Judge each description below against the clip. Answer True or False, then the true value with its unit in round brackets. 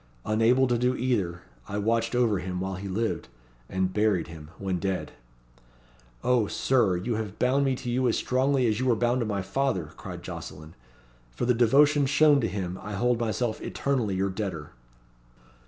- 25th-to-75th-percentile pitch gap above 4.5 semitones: True (4.9 semitones)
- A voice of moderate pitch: False (110 Hz)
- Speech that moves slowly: False (180 wpm)